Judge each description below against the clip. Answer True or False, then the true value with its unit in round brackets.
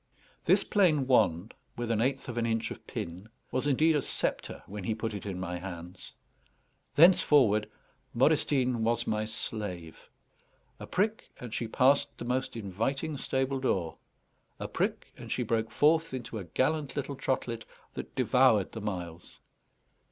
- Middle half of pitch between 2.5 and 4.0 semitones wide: False (4.6 semitones)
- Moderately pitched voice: False (115 Hz)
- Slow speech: False (155 wpm)